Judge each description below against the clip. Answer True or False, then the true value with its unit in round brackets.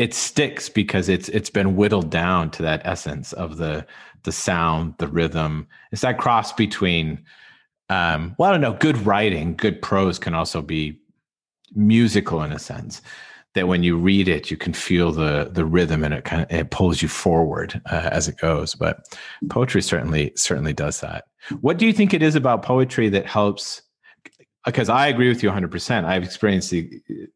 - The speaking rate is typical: True (190 wpm)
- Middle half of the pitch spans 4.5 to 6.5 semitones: False (4.1 semitones)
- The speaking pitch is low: True (90 Hz)